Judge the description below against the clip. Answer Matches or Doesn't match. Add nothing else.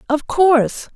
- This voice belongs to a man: Doesn't match